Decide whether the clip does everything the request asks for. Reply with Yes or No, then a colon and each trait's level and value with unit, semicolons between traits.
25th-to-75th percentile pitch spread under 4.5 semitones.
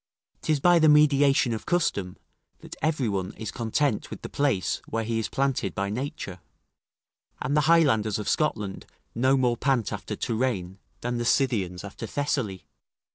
No: wide, 5.5 semitones